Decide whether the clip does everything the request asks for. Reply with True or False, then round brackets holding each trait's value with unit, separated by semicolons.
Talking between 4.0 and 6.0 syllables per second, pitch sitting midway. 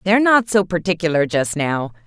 True (5.5 syllables/s; 175 Hz)